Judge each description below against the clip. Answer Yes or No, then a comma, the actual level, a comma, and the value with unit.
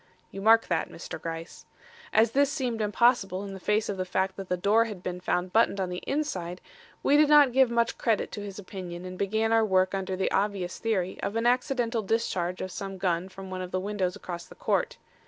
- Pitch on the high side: Yes, high, 195 Hz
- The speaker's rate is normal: No, fast, 220 wpm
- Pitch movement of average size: Yes, average, 3.7 semitones